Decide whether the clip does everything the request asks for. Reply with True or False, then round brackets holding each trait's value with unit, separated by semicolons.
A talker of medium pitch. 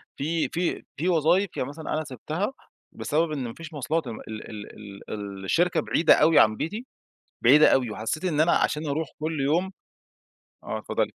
True (155 Hz)